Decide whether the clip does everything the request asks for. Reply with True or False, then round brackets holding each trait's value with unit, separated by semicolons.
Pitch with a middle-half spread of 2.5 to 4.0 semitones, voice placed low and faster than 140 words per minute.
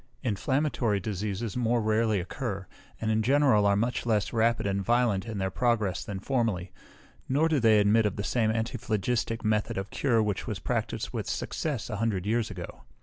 True (2.8 semitones; 110 Hz; 180 wpm)